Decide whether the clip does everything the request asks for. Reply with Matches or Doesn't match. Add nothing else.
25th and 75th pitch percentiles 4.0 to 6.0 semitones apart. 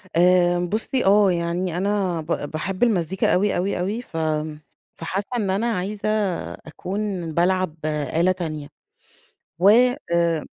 Doesn't match